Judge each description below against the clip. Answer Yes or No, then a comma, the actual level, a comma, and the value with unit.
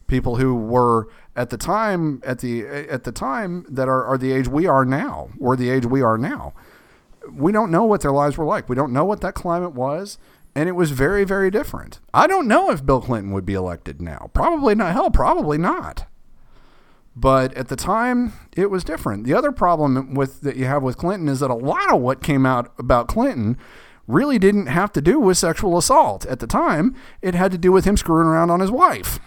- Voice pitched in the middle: Yes, medium, 145 Hz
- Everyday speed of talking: No, fast, 225 wpm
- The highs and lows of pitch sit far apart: Yes, wide, 6.1 semitones